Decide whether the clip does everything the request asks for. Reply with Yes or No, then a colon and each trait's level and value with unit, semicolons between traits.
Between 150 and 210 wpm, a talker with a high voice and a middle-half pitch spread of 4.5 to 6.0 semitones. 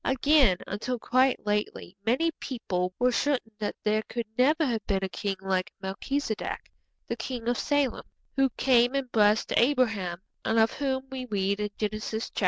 No: average, 170 wpm; high, 230 Hz; average, 4.1 semitones